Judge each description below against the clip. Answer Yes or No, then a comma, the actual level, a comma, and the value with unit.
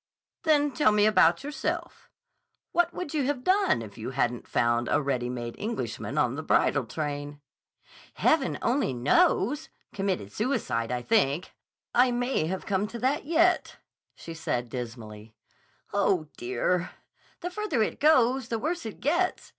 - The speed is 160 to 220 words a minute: No, average, 150 wpm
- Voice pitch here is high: Yes, high, 210 Hz